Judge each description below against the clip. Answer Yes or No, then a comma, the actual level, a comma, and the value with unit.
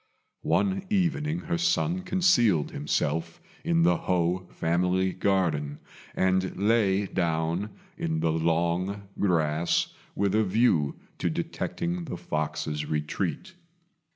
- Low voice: Yes, very low, 95 Hz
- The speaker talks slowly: Yes, slow, 110 wpm